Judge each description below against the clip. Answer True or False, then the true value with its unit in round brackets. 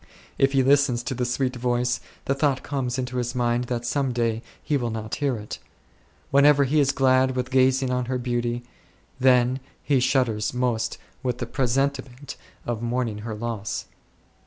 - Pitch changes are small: True (1.8 semitones)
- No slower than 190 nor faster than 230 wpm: False (170 wpm)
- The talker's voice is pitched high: False (125 Hz)